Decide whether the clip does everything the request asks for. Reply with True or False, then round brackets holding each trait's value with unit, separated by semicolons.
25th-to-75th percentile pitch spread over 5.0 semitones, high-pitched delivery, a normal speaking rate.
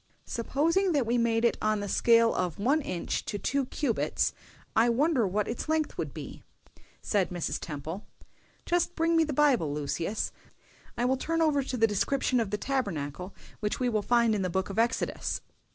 True (5.6 semitones; 230 Hz; 185 wpm)